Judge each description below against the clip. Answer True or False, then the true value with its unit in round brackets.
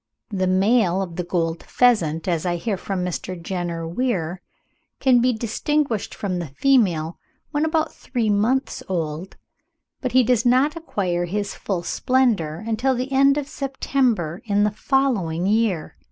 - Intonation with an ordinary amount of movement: False (6.5 semitones)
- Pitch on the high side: True (205 Hz)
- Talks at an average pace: True (155 wpm)